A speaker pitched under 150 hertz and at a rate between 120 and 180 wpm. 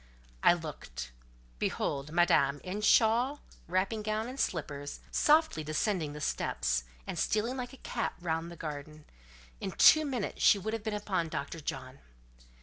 No: medium, 175 Hz; average, 150 wpm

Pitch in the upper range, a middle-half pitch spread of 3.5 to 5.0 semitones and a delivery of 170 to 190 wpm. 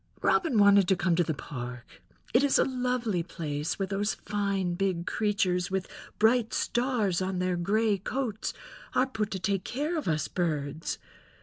No: high, 195 Hz; average, 4.1 semitones; average, 160 wpm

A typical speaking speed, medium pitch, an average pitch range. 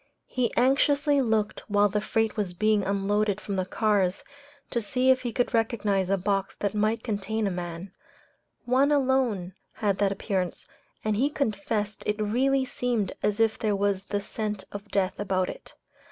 No: average, 170 wpm; high, 210 Hz; average, 3.0 semitones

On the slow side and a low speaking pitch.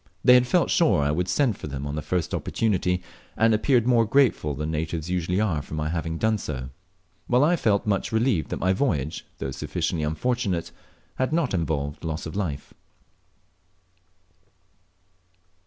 No: average, 165 wpm; very low, 90 Hz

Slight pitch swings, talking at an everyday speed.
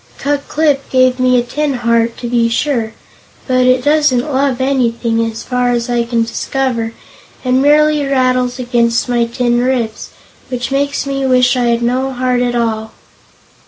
Yes: narrow, 2.2 semitones; average, 165 wpm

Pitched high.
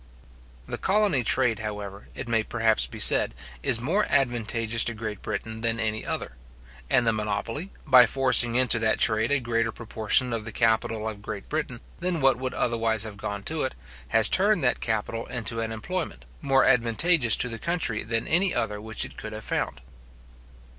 No: low, 115 Hz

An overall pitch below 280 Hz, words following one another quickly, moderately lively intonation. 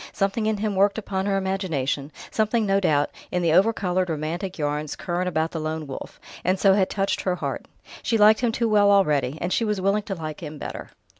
Yes: high, 190 Hz; fast, 215 wpm; average, 4.3 semitones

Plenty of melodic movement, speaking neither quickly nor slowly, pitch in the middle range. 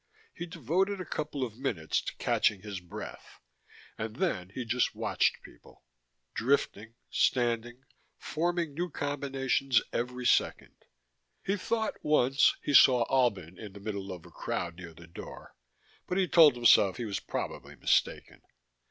No: wide, 6.4 semitones; average, 145 wpm; low, 125 Hz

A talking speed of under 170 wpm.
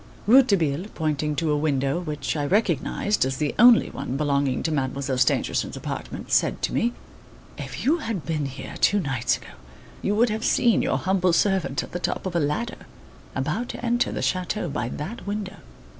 No: average, 185 wpm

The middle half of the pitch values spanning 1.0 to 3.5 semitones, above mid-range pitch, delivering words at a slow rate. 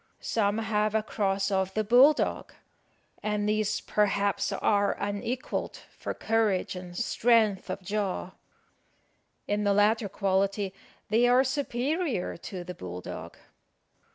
Yes: narrow, 2.5 semitones; high, 205 Hz; slow, 125 wpm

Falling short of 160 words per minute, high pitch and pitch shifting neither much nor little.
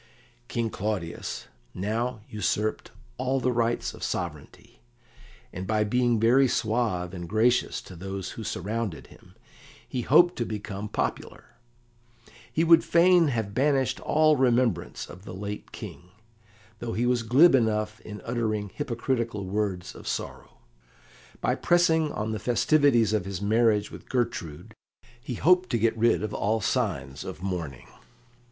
No: average, 145 wpm; low, 110 Hz; average, 3.7 semitones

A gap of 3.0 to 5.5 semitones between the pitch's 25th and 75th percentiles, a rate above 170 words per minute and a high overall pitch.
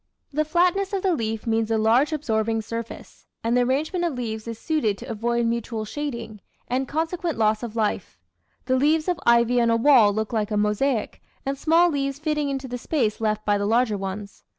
Yes: average, 5.1 semitones; average, 195 wpm; high, 235 Hz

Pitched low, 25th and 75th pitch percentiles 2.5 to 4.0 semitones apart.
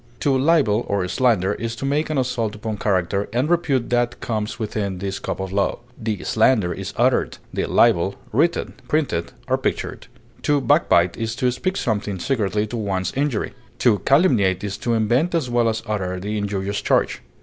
No: low, 110 Hz; average, 4.4 semitones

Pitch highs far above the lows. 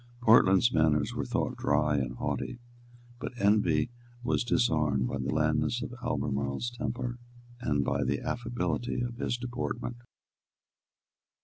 Yes: wide, 8.2 semitones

